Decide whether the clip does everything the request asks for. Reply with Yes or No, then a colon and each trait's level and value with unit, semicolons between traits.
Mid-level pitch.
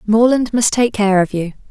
No: high, 215 Hz